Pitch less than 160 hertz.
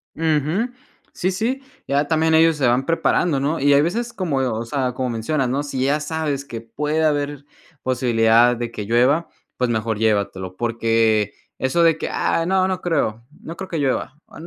Yes: medium, 140 Hz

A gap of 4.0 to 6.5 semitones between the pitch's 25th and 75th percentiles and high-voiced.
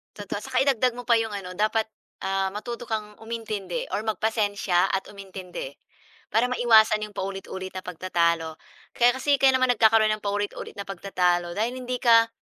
No: average, 3.2 semitones; high, 210 Hz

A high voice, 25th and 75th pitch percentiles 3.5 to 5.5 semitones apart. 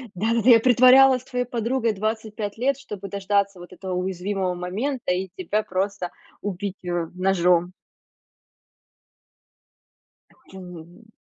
Yes: high, 200 Hz; average, 4.0 semitones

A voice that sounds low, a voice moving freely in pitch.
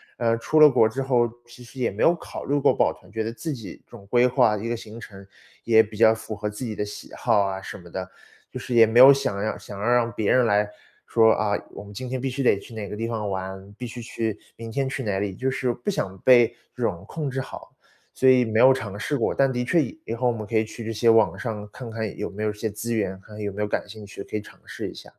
No: low, 115 Hz; average, 3.0 semitones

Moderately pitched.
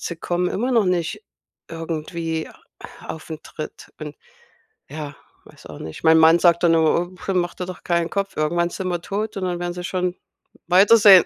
Yes: medium, 175 Hz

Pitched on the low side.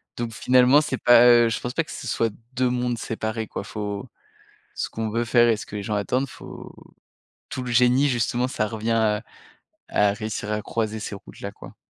Yes: low, 115 Hz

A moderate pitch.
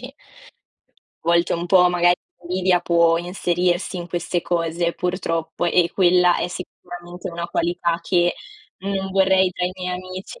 Yes: medium, 175 Hz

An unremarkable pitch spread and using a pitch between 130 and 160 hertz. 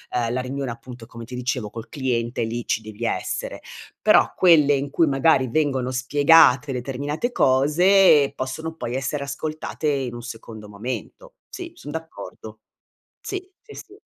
Yes: average, 4.2 semitones; low, 135 Hz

